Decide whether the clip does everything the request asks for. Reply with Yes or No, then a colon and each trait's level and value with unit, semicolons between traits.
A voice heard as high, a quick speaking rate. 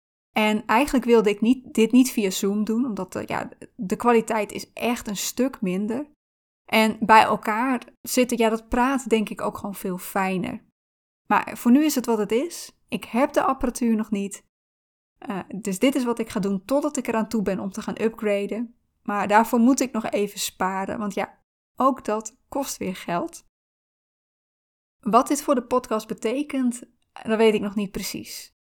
No: high, 220 Hz; average, 190 wpm